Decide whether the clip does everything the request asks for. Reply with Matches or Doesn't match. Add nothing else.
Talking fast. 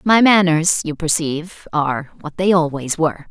Doesn't match